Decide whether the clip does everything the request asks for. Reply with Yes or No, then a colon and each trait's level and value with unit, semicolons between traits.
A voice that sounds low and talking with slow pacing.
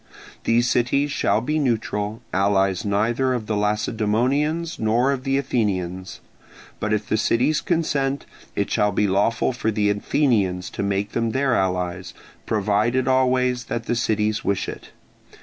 No: low, 110 Hz; average, 150 wpm